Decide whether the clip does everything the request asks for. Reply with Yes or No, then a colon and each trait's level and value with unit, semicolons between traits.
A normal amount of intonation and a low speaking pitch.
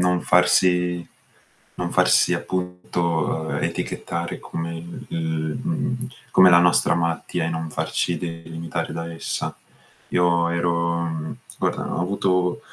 No: narrow, 1.4 semitones; very low, 85 Hz